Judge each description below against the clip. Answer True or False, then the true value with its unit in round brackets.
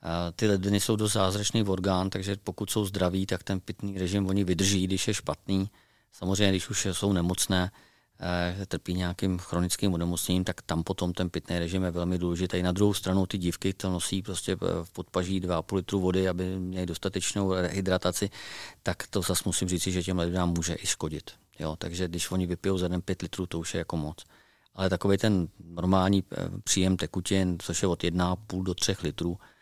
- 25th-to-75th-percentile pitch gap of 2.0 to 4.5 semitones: False (1.5 semitones)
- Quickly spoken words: True (190 wpm)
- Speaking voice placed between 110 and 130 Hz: False (95 Hz)